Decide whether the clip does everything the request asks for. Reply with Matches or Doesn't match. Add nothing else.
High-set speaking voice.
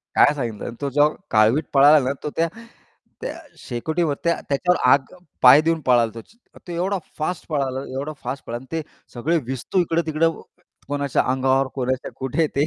Doesn't match